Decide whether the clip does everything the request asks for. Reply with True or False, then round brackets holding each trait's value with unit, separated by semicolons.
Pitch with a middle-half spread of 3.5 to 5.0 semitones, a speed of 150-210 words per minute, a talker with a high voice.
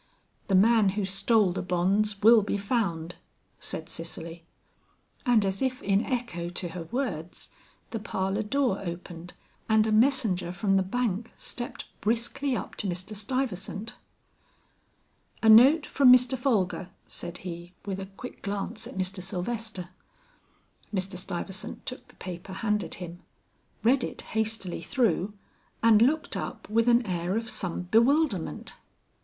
False (4.2 semitones; 140 wpm; 205 Hz)